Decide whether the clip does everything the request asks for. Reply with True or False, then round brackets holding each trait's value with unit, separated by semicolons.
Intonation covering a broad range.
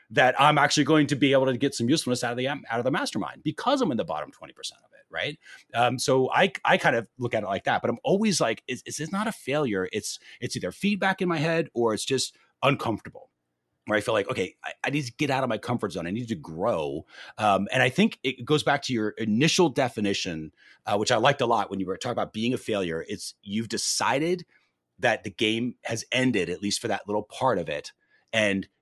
True (5.7 semitones)